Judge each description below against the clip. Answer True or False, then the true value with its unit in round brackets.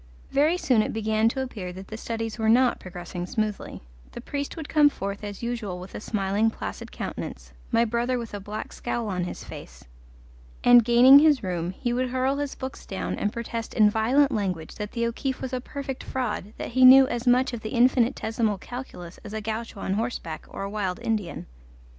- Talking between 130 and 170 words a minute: False (200 wpm)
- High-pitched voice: True (225 Hz)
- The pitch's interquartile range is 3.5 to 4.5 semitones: True (3.8 semitones)